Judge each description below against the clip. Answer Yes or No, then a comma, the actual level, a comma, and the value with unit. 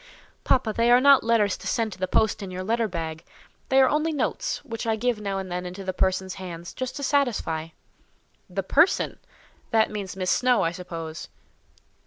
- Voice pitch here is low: No, high, 205 Hz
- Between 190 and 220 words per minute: Yes, average, 195 wpm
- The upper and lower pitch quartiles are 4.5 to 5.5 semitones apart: Yes, average, 5.0 semitones